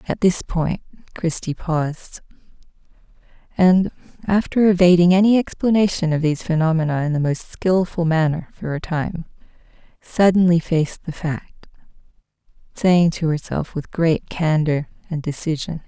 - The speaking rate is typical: No, slow, 125 wpm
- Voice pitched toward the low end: No, medium, 170 Hz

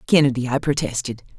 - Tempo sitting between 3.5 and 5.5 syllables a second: No, 6.3 syllables/s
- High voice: No, low, 130 Hz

